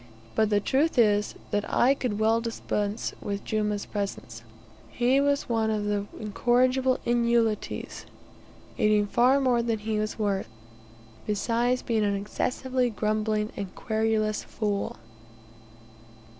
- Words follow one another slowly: Yes, slow, 125 wpm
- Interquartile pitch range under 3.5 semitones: Yes, narrow, 2.6 semitones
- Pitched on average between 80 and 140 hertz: No, high, 220 Hz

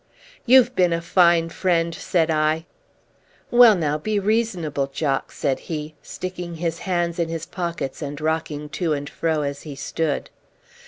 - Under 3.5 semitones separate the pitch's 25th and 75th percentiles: Yes, average, 2.7 semitones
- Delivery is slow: No, average, 155 wpm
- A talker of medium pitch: Yes, medium, 165 Hz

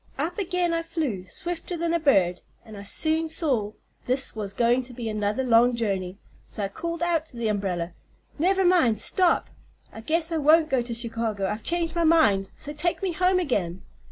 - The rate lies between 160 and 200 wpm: Yes, average, 195 wpm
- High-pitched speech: Yes, very high, 260 Hz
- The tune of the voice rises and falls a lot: Yes, wide, 7.9 semitones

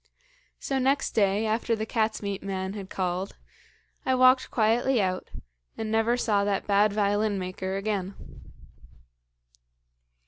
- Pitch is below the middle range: No, high, 210 Hz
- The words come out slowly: Yes, slow, 130 wpm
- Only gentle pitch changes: Yes, narrow, 2.3 semitones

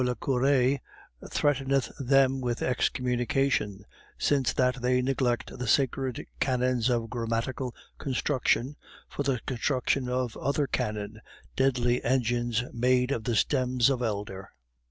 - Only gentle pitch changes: Yes, narrow, 2.0 semitones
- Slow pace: Yes, slow, 120 wpm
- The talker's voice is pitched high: No, low, 125 Hz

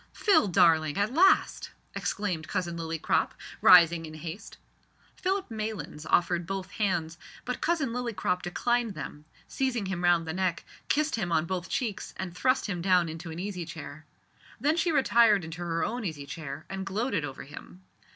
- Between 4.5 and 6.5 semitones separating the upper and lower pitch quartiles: Yes, wide, 5.4 semitones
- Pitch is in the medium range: Yes, medium, 180 Hz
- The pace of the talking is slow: No, average, 165 wpm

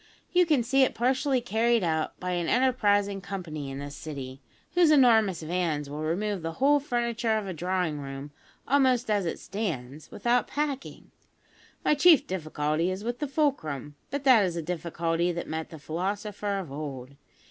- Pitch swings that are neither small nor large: No, wide, 7.5 semitones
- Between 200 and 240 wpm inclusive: No, average, 170 wpm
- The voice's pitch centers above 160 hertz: Yes, high, 190 Hz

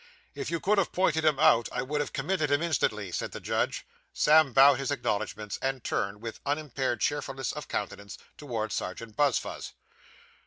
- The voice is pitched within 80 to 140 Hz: Yes, low, 135 Hz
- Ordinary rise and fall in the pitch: Yes, average, 4.9 semitones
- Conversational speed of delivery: Yes, average, 170 wpm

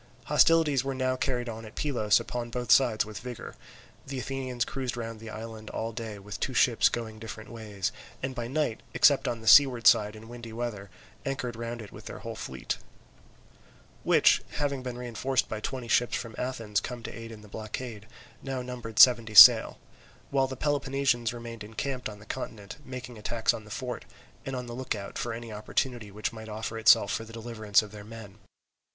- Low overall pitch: Yes, low, 115 Hz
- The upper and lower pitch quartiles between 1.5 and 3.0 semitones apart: Yes, narrow, 2.6 semitones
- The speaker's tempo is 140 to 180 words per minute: No, average, 195 wpm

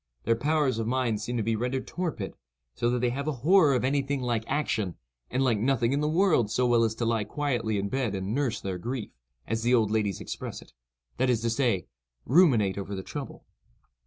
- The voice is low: Yes, low, 120 Hz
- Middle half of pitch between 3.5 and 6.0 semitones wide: Yes, average, 3.8 semitones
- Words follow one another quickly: Yes, fast, 220 wpm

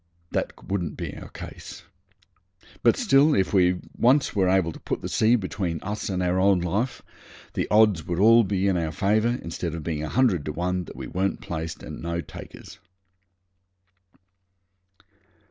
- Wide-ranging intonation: No, average, 4.1 semitones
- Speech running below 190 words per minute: Yes, average, 170 wpm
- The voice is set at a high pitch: No, very low, 95 Hz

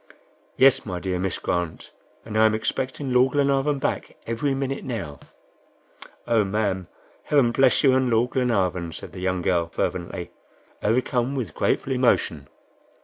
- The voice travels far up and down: Yes, wide, 6.0 semitones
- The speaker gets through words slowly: No, average, 145 wpm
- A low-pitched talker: Yes, low, 115 Hz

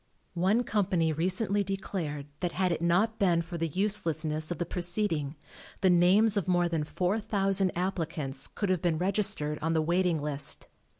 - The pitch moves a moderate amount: Yes, average, 3.3 semitones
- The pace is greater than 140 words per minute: Yes, average, 165 wpm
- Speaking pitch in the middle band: Yes, medium, 175 Hz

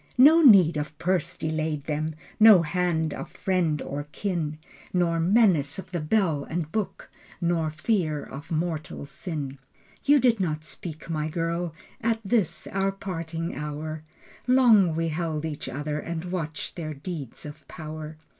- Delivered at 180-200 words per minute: No, average, 150 wpm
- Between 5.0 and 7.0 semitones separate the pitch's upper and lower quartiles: No, average, 3.2 semitones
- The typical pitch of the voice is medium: Yes, medium, 165 Hz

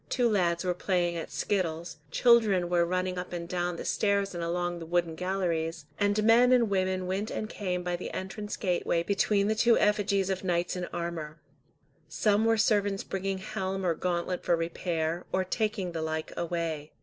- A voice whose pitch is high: No, medium, 180 Hz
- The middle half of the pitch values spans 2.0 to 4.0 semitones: Yes, average, 2.8 semitones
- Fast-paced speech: No, average, 185 wpm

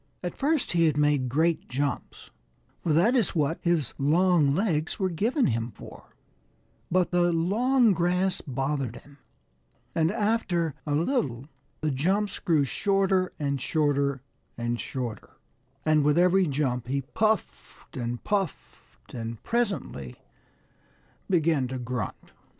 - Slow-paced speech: Yes, slow, 130 wpm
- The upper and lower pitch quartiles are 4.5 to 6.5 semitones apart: Yes, wide, 5.4 semitones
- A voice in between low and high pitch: Yes, medium, 155 Hz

